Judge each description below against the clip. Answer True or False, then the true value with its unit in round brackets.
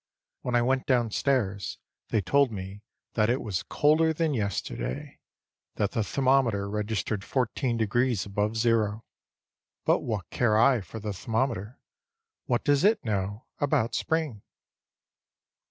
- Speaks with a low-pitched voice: True (115 Hz)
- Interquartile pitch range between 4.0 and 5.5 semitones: True (4.3 semitones)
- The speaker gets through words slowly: True (130 wpm)